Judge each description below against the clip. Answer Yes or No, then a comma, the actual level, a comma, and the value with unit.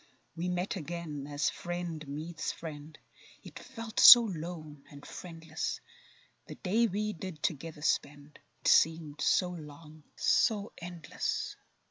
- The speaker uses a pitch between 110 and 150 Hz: No, medium, 165 Hz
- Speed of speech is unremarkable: No, slow, 120 wpm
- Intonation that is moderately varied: Yes, average, 3.1 semitones